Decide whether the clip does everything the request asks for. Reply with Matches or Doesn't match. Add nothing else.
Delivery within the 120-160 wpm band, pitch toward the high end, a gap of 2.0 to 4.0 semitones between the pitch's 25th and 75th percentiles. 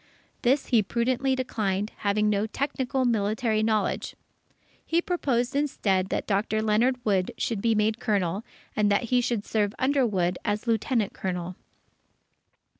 Matches